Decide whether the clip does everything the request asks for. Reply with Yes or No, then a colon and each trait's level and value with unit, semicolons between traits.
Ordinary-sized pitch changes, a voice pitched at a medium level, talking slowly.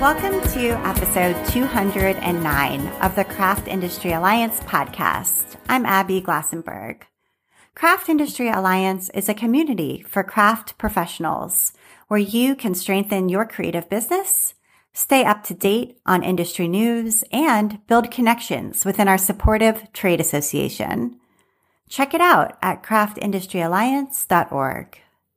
No: average, 4.3 semitones; high, 210 Hz; slow, 115 wpm